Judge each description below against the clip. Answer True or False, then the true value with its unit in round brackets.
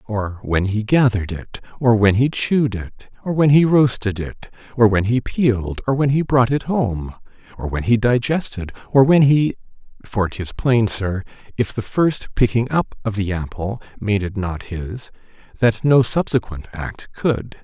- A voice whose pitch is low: True (115 Hz)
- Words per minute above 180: False (170 wpm)